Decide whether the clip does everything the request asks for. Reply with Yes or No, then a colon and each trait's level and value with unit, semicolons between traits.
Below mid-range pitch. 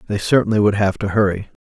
Yes: low, 105 Hz